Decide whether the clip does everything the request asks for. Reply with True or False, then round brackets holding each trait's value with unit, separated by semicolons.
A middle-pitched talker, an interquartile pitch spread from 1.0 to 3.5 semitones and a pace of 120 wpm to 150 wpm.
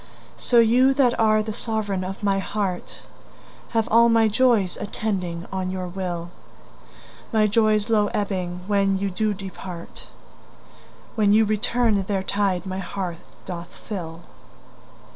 False (200 Hz; 2.8 semitones; 135 wpm)